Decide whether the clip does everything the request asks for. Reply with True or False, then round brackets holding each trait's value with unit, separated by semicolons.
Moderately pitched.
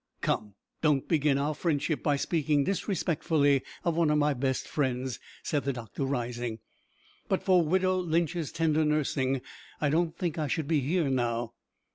True (150 Hz)